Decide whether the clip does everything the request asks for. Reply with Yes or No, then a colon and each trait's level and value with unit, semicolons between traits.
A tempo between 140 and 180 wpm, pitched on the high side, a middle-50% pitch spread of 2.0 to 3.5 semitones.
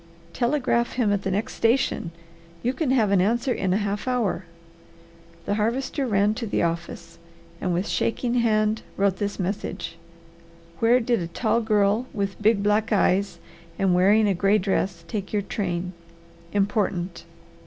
Yes: average, 155 wpm; high, 205 Hz; average, 3.1 semitones